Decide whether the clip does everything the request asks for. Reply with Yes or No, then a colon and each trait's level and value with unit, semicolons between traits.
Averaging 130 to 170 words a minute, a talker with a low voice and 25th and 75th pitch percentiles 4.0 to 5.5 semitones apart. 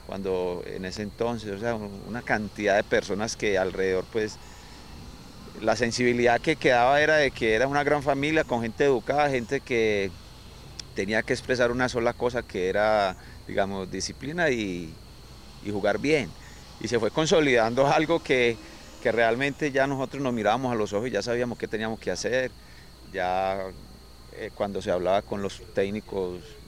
Yes: average, 165 wpm; low, 115 Hz; average, 5.1 semitones